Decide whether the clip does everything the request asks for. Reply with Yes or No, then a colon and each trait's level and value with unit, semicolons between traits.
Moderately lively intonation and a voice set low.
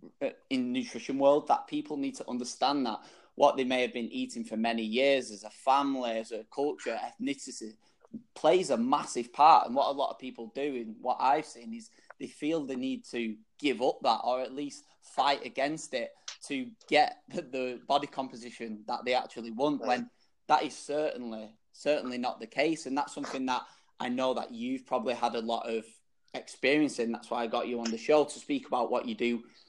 Yes: average, 4.1 semitones; low, 130 Hz